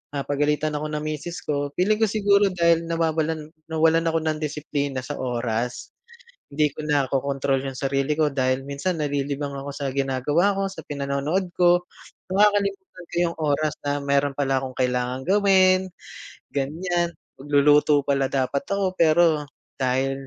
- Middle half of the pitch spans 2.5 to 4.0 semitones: Yes, average, 3.4 semitones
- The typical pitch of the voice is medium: Yes, medium, 150 Hz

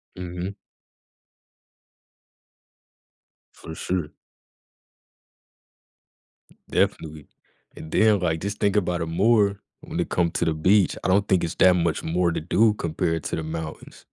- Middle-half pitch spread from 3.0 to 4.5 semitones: Yes, average, 3.4 semitones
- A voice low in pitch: Yes, very low, 90 Hz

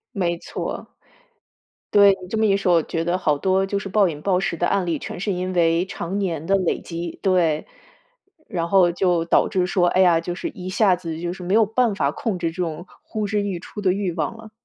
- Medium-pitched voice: Yes, medium, 180 Hz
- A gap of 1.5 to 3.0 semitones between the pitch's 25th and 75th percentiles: Yes, narrow, 2.6 semitones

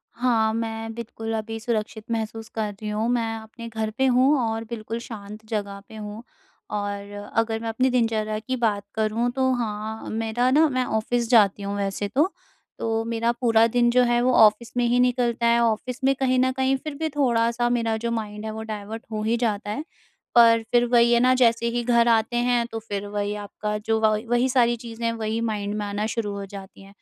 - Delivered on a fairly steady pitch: Yes, narrow, 1.9 semitones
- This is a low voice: No, high, 225 Hz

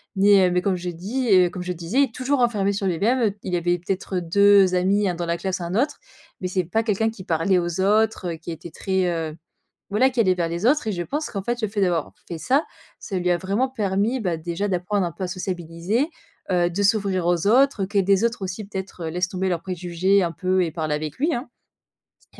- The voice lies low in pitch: No, high, 190 Hz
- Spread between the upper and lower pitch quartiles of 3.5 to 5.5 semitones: No, average, 3.1 semitones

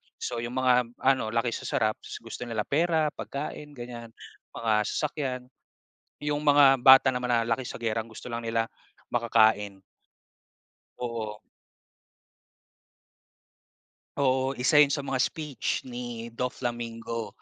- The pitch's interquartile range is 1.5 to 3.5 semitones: Yes, average, 2.7 semitones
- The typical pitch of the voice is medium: No, low, 120 Hz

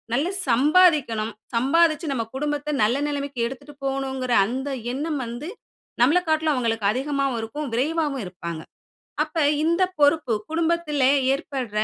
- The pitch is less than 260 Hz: No, very high, 280 Hz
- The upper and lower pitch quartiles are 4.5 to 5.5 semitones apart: No, average, 3.8 semitones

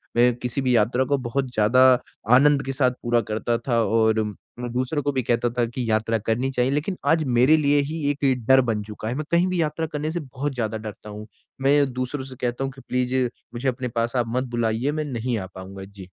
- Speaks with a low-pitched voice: Yes, low, 125 Hz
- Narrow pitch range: No, average, 3.1 semitones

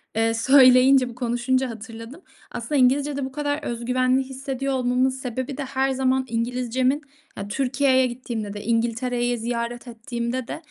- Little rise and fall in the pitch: Yes, narrow, 2.0 semitones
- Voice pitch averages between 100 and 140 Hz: No, very high, 255 Hz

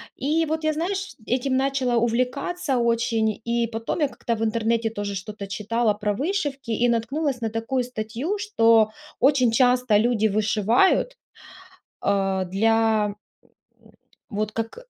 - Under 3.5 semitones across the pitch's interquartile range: No, average, 3.8 semitones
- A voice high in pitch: Yes, high, 230 Hz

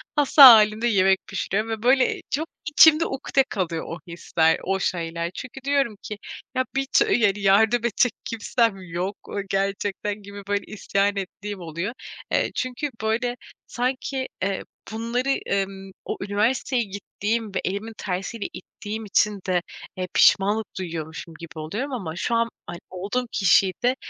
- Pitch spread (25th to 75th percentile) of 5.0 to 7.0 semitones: No, average, 3.9 semitones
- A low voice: No, high, 205 Hz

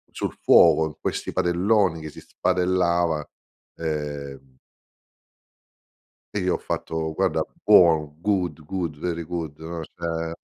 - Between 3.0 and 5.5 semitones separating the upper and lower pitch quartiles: No, narrow, 2.4 semitones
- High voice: No, very low, 80 Hz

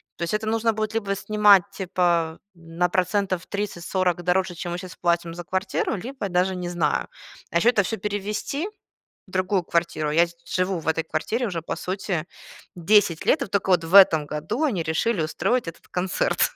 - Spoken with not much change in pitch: No, average, 3.3 semitones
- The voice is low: No, medium, 185 Hz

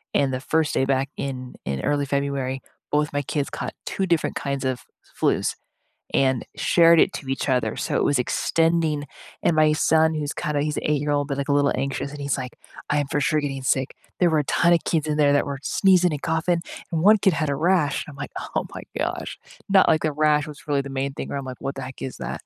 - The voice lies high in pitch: No, medium, 145 Hz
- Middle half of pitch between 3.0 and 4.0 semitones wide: No, narrow, 2.4 semitones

